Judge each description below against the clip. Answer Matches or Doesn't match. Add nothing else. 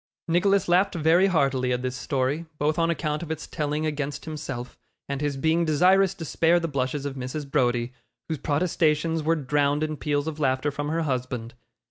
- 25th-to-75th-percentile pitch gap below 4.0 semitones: Matches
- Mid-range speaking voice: Matches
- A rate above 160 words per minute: Matches